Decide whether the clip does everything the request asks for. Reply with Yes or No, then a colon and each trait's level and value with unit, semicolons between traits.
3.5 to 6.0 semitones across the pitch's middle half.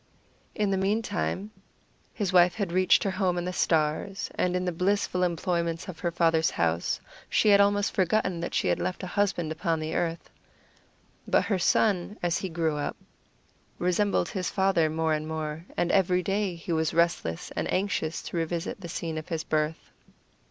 No: average, 2.9 semitones